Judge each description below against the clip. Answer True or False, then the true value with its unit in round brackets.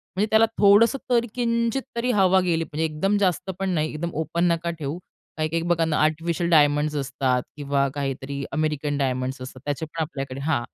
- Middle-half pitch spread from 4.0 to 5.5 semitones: True (4.3 semitones)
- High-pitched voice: False (155 Hz)